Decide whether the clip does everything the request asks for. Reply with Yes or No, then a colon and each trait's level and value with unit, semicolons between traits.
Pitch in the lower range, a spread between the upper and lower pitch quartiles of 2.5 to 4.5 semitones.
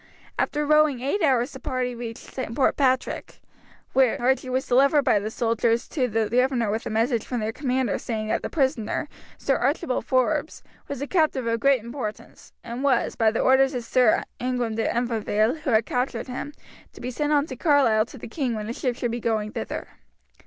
No: very high, 250 Hz; average, 2.9 semitones